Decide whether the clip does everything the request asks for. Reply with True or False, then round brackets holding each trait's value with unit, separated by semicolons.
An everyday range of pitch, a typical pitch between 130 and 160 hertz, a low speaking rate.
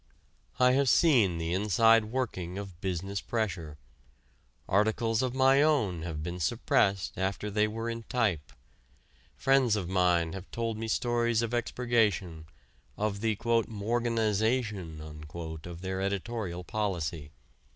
False (4.6 semitones; 105 Hz; 125 wpm)